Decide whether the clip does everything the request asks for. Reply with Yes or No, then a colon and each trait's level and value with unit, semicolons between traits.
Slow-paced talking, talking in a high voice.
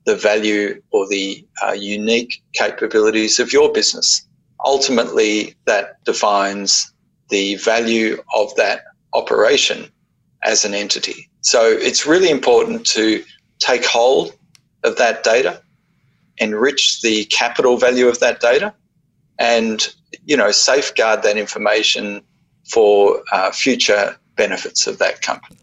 No: slow, 120 wpm; low, 120 Hz